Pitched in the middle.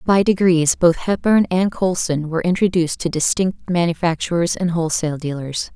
Yes: medium, 170 Hz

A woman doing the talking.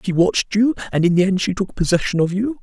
No: male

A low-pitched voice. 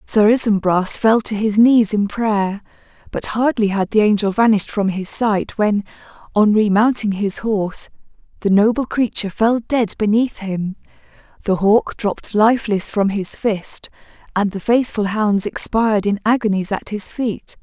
No: high, 210 Hz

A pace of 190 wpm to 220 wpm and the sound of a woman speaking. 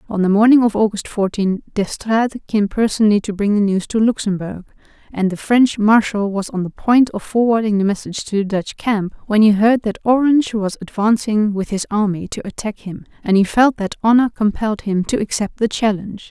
Yes: average, 200 wpm; female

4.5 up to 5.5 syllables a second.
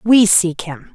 No: 3.3 syllables/s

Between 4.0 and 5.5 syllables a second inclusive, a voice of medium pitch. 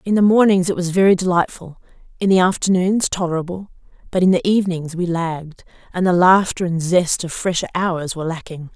No: 5.7 syllables/s; medium, 180 Hz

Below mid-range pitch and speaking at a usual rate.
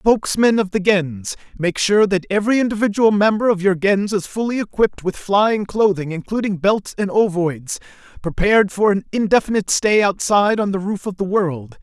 No: high, 200 Hz; average, 175 wpm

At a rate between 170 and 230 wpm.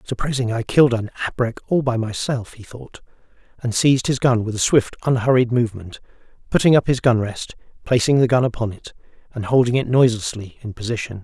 Yes: average, 185 wpm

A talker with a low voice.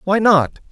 No: high, 190 Hz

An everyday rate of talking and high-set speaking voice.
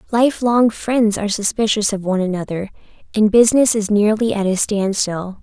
Yes: average, 155 wpm; high, 210 Hz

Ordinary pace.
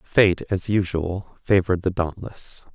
No: slow, 130 wpm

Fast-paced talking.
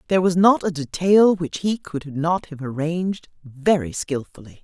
No: average, 170 wpm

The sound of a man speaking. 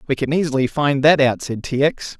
Yes: male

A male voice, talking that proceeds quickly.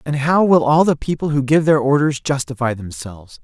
Yes: male; fast, 210 wpm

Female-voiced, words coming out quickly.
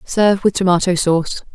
No: female; average, 155 wpm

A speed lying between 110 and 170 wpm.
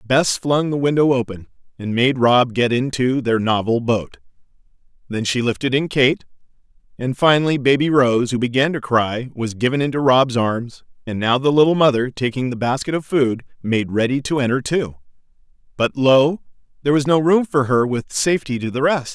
No: average, 185 wpm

